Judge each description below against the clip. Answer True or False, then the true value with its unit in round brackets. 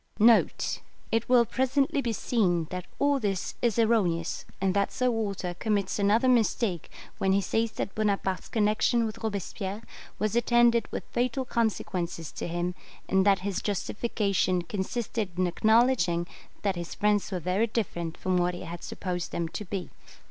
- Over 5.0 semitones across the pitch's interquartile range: False (4.1 semitones)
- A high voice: True (205 Hz)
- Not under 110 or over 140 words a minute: False (155 wpm)